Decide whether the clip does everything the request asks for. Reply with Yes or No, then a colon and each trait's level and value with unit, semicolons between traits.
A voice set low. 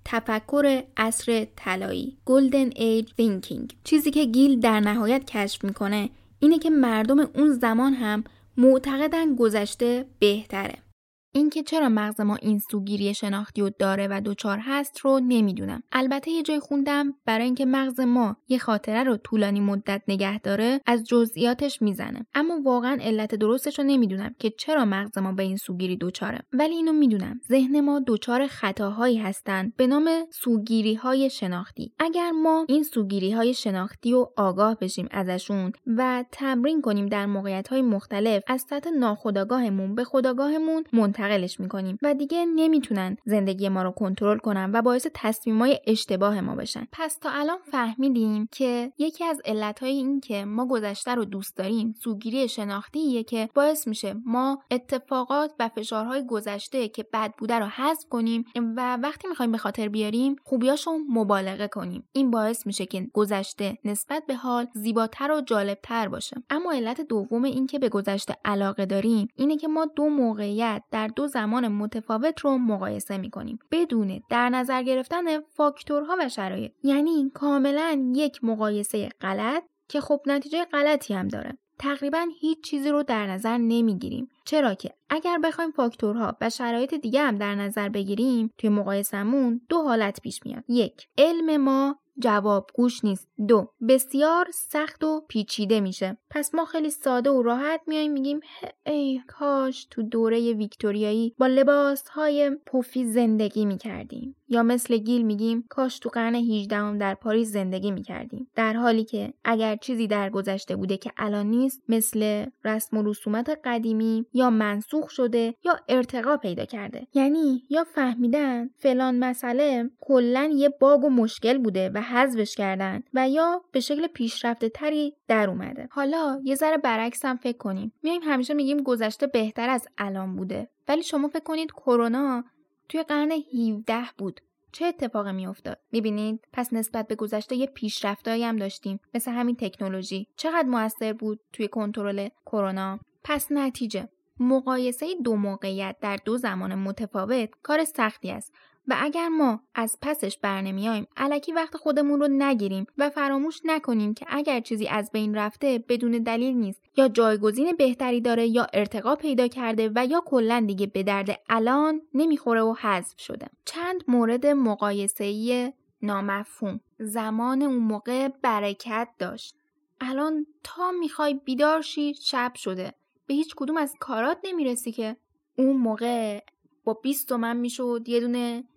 No: high, 240 Hz